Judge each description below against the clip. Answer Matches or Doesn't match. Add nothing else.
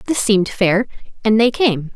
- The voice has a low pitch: Doesn't match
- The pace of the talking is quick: Doesn't match